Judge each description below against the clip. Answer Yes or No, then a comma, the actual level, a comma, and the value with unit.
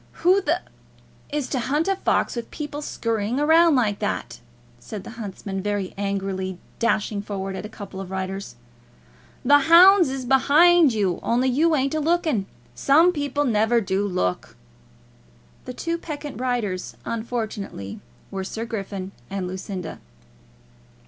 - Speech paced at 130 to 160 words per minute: Yes, average, 140 wpm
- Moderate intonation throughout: No, wide, 6.8 semitones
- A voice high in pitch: Yes, high, 230 Hz